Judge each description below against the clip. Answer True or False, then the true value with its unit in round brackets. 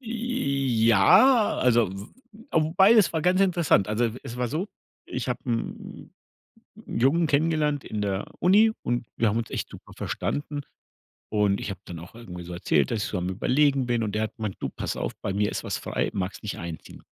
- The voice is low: True (120 Hz)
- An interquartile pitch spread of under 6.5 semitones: False (7.2 semitones)